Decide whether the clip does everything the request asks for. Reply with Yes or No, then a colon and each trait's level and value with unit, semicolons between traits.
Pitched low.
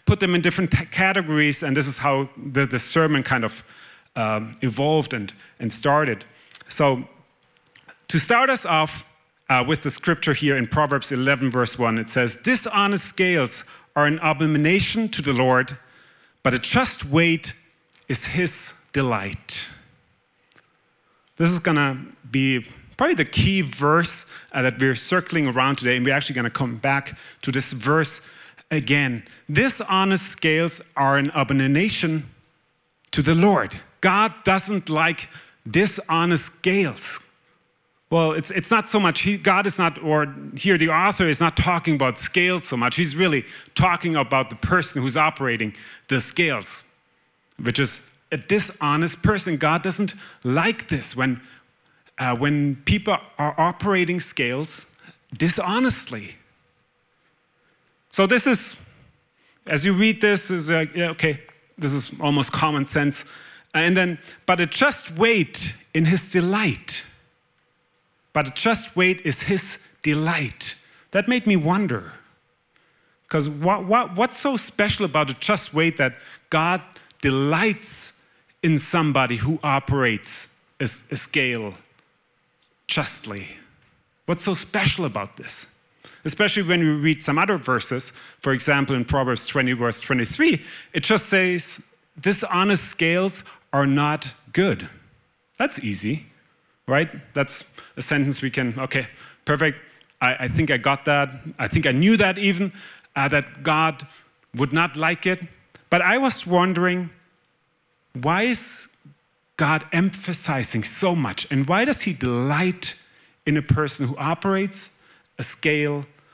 No: medium, 155 Hz